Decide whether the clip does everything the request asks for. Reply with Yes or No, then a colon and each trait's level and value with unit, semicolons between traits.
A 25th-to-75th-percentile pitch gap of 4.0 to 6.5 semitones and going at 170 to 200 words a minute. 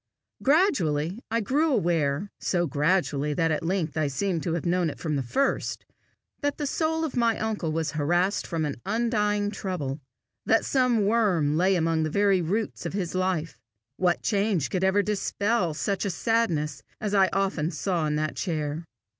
Yes: average, 4.9 semitones; average, 175 wpm